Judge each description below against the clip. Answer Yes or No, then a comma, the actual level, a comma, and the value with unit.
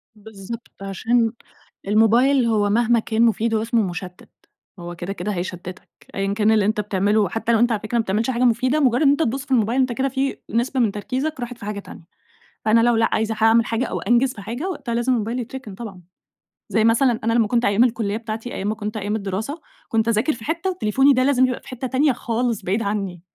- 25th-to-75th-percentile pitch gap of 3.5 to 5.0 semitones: No, average, 2.9 semitones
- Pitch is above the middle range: Yes, high, 225 Hz